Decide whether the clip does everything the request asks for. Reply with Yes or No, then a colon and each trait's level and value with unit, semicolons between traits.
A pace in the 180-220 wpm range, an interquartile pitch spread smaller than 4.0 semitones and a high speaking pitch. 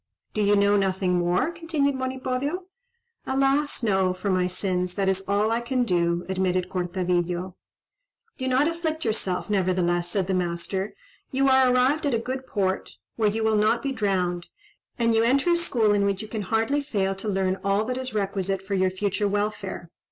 No: average, 185 wpm; wide, 5.4 semitones; high, 205 Hz